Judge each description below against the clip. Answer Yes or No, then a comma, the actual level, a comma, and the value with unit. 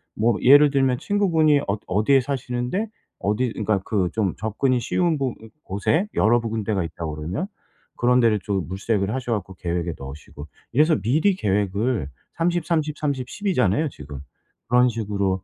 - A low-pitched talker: Yes, low, 115 Hz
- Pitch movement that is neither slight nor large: No, wide, 6.3 semitones